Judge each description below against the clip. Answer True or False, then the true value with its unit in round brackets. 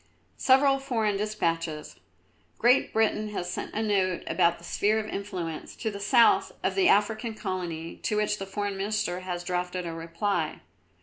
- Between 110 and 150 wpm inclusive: False (165 wpm)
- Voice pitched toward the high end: True (200 Hz)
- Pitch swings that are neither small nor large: True (3.4 semitones)